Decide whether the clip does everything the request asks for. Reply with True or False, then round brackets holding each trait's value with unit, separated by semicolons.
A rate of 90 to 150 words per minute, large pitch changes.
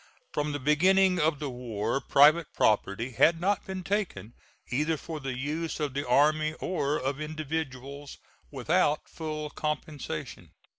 False (140 wpm; 3.0 semitones)